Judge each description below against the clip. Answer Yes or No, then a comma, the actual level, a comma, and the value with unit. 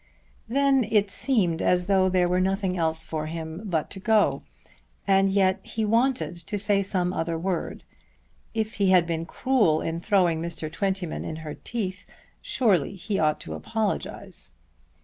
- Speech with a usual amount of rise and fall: Yes, average, 3.7 semitones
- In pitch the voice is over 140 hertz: Yes, medium, 185 Hz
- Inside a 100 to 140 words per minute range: No, average, 160 wpm